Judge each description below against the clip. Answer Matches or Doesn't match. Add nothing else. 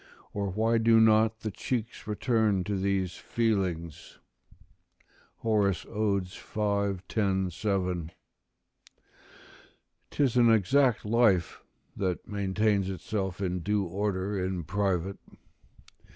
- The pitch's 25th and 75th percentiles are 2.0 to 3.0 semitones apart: Matches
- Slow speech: Matches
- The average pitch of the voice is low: Matches